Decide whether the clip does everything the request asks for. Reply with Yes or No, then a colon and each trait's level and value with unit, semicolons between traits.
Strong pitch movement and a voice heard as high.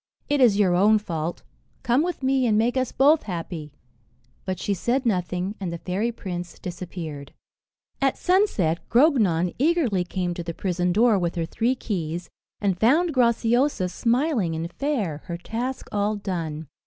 Yes: wide, 6.1 semitones; high, 200 Hz